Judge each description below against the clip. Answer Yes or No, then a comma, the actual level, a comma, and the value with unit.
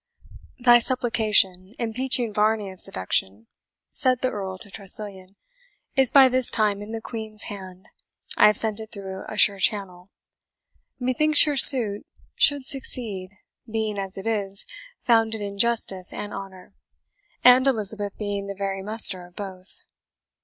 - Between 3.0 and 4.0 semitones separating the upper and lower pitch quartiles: Yes, average, 3.3 semitones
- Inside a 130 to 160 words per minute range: Yes, average, 145 wpm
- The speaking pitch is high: Yes, high, 210 Hz